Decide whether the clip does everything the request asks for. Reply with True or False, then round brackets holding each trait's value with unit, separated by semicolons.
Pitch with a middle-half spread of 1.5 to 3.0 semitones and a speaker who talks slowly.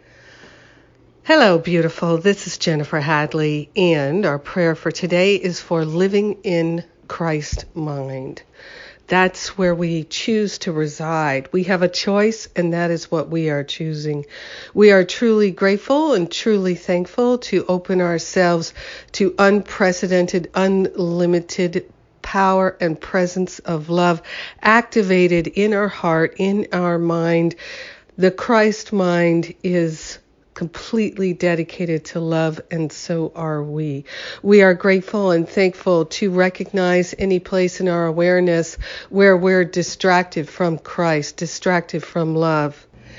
True (2.5 semitones; 125 wpm)